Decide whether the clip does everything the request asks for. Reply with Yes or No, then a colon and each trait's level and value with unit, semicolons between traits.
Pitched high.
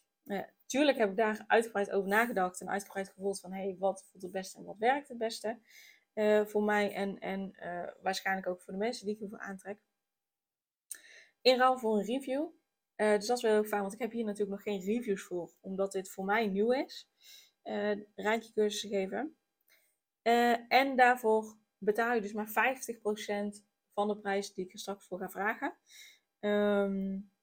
Yes: high, 210 Hz